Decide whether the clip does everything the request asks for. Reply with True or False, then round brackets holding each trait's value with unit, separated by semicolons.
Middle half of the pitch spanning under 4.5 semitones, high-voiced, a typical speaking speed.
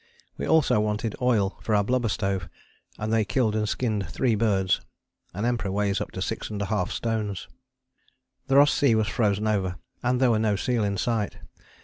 False (2.7 semitones; 110 Hz; 180 wpm)